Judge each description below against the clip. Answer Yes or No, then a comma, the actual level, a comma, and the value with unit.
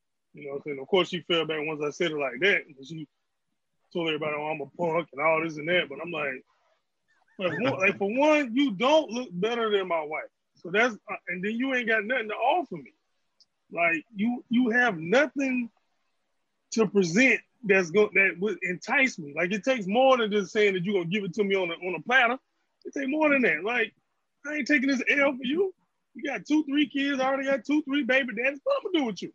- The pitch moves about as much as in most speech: No, wide, 7.1 semitones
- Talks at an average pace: No, fast, 240 wpm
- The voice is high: Yes, high, 215 Hz